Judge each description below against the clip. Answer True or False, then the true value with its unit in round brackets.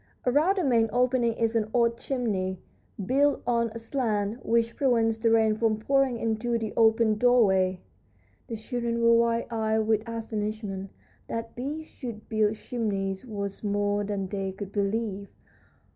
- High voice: True (225 Hz)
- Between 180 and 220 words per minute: False (150 wpm)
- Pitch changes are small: True (2.2 semitones)